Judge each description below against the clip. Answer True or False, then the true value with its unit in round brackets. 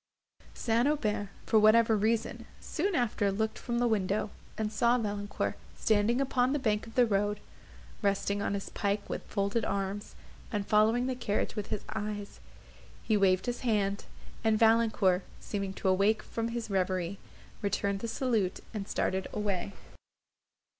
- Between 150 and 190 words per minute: True (155 wpm)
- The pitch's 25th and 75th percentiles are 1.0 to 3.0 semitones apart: True (2.4 semitones)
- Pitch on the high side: True (210 Hz)